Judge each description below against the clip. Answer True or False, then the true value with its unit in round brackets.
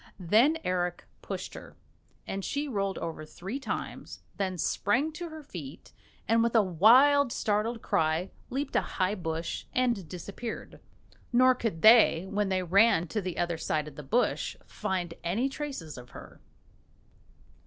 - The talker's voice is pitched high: True (200 Hz)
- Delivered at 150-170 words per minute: True (155 wpm)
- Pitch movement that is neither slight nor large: False (5.8 semitones)